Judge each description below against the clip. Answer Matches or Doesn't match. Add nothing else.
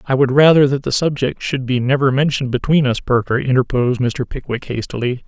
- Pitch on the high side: Doesn't match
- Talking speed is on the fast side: Doesn't match